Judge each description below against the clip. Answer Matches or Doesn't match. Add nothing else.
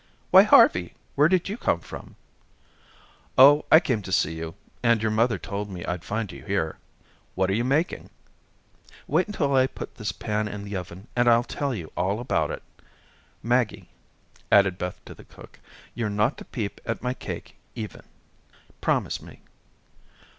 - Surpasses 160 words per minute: Matches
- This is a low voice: Matches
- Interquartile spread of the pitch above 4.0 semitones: Matches